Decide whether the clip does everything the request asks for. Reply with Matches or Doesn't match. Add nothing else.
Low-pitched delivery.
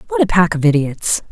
Doesn't match